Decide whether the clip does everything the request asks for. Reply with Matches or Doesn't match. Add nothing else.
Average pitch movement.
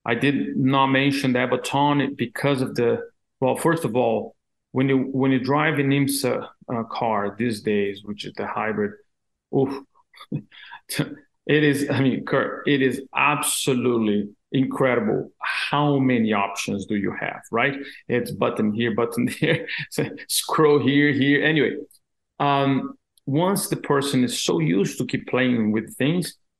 Matches